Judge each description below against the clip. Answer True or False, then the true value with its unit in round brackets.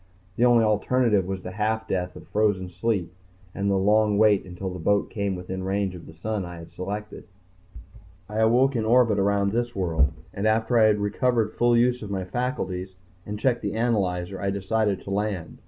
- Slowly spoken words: False (190 wpm)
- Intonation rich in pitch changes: False (2.9 semitones)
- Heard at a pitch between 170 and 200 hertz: False (105 Hz)